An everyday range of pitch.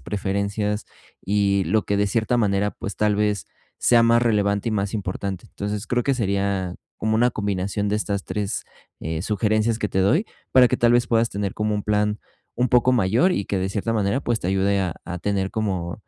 No: narrow, 2.3 semitones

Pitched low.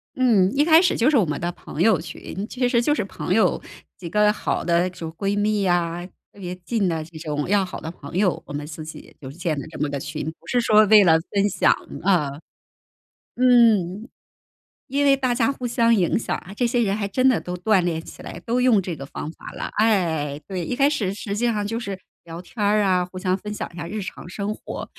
No: high, 195 Hz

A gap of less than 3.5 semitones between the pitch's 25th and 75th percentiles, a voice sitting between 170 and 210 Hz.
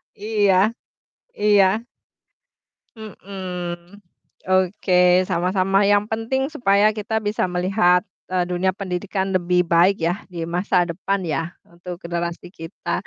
Yes: narrow, 2.5 semitones; medium, 185 Hz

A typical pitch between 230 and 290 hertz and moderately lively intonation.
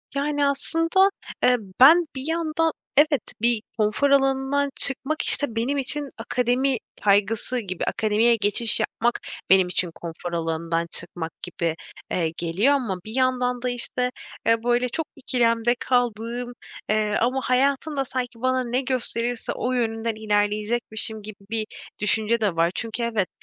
Yes: high, 240 Hz; average, 3.9 semitones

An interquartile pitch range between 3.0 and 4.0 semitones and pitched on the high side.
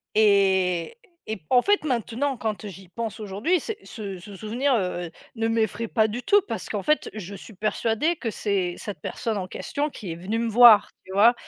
Yes: average, 3.5 semitones; high, 220 Hz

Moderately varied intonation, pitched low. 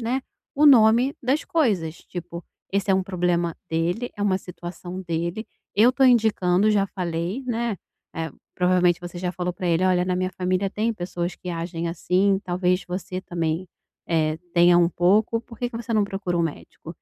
No: average, 3.6 semitones; medium, 185 Hz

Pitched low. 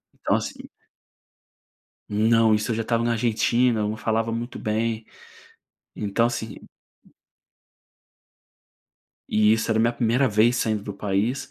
Yes: low, 115 Hz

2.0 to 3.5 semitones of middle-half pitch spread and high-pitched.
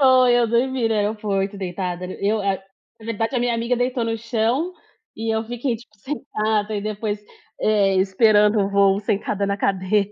Yes: average, 2.7 semitones; high, 215 Hz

